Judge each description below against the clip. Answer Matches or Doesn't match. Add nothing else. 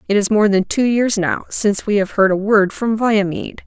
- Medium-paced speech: Doesn't match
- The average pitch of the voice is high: Matches